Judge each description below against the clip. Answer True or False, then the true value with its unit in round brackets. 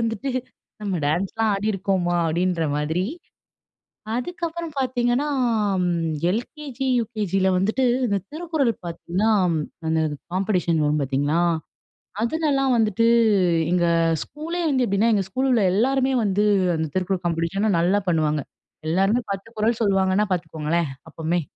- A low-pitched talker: False (195 Hz)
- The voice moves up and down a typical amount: False (5.8 semitones)